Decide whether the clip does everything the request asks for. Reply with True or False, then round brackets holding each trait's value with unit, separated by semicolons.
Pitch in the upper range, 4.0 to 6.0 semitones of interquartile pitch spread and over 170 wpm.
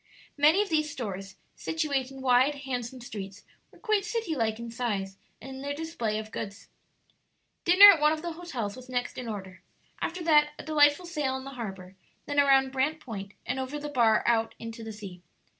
True (265 Hz; 5.1 semitones; 195 wpm)